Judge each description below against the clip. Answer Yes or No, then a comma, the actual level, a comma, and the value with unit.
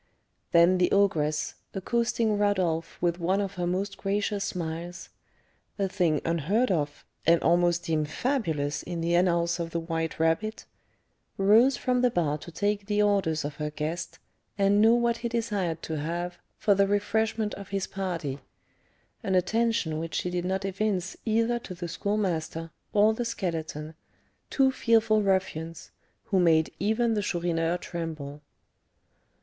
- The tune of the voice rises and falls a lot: No, average, 4.0 semitones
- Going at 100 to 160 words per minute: Yes, average, 150 wpm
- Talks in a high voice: No, medium, 180 Hz